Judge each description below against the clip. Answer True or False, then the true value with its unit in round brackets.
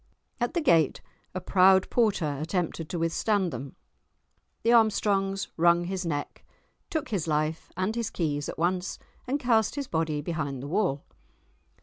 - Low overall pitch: False (180 Hz)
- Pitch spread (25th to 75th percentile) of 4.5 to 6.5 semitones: True (5.1 semitones)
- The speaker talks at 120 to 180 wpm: True (150 wpm)